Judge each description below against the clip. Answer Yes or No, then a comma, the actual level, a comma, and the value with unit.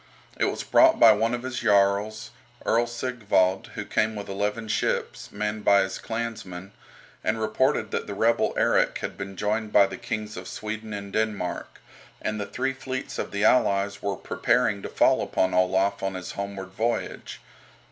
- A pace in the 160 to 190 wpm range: Yes, average, 175 wpm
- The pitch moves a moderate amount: No, narrow, 2.2 semitones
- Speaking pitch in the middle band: No, low, 105 Hz